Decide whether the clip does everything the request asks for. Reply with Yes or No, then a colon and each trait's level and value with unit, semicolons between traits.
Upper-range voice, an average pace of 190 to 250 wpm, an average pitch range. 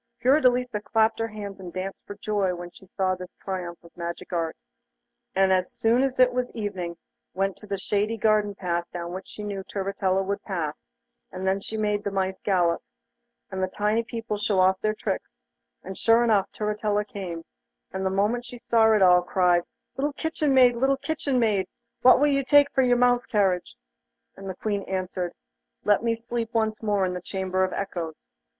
Yes: high, 205 Hz; average, 195 wpm; average, 3.4 semitones